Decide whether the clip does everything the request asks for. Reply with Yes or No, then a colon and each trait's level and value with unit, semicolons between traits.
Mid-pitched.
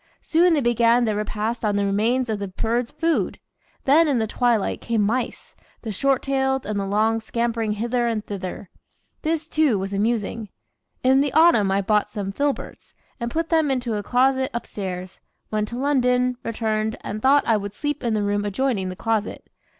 No: high, 230 Hz